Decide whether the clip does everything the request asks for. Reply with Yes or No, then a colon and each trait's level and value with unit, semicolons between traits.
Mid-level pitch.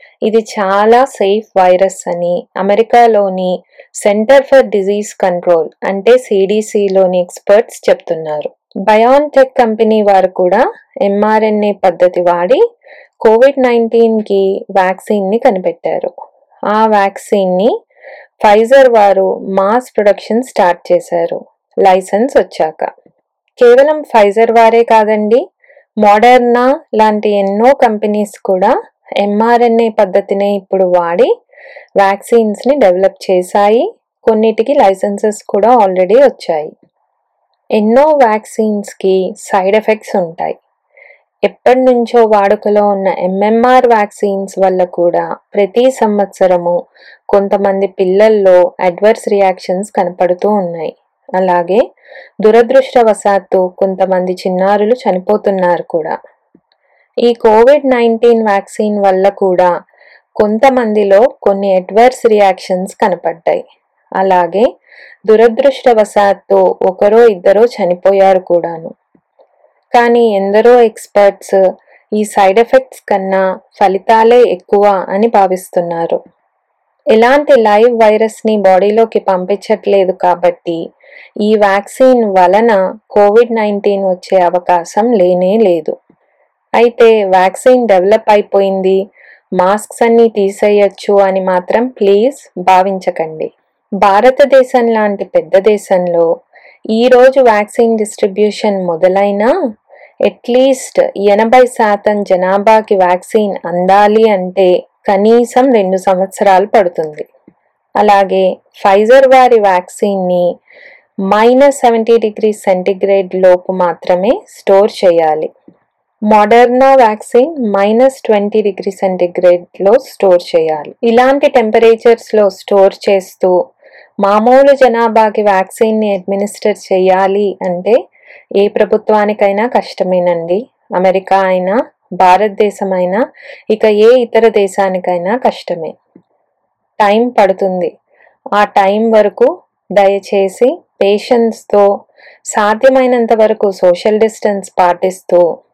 No: high, 205 Hz